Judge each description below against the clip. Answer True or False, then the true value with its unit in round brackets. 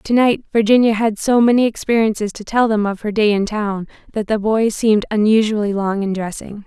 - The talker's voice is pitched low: False (215 Hz)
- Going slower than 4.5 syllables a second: False (5.5 syllables/s)